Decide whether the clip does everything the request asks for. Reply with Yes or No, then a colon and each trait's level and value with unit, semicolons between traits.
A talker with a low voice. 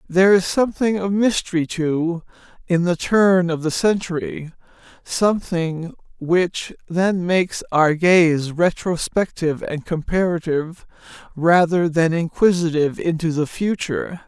No: medium, 175 Hz